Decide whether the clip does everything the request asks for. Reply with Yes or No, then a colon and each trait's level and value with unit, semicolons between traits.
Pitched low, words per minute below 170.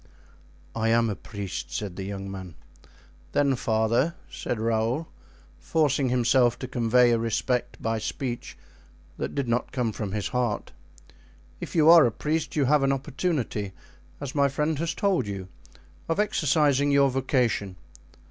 Yes: low, 125 Hz; average, 150 wpm